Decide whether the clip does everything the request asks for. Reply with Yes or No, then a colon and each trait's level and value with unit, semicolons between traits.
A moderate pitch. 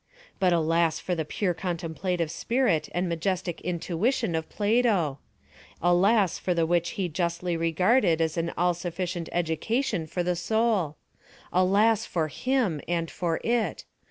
Yes: medium, 175 Hz